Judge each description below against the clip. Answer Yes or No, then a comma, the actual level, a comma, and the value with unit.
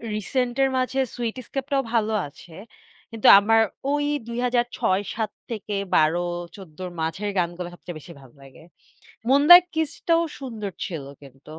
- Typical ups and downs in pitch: No, wide, 6.3 semitones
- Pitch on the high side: Yes, high, 210 Hz